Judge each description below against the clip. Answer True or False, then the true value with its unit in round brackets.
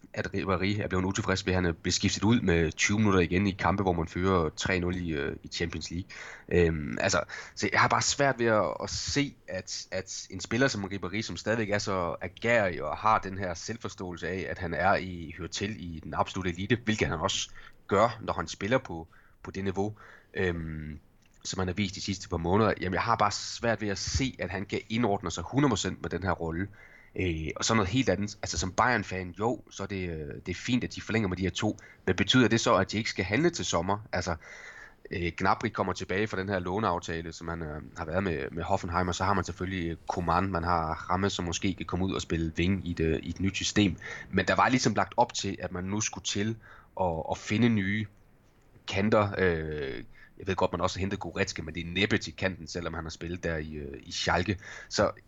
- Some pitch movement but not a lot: True (3.3 semitones)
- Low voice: True (95 Hz)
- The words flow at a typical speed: False (235 wpm)